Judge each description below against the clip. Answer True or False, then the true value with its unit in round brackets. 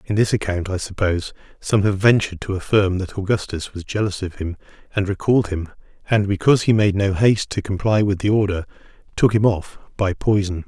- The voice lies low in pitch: True (100 Hz)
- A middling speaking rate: True (195 wpm)